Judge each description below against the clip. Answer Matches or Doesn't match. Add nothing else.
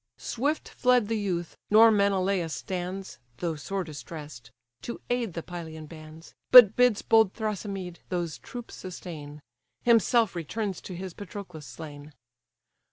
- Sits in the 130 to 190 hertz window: Matches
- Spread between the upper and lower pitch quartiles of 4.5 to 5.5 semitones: Matches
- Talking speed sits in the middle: Doesn't match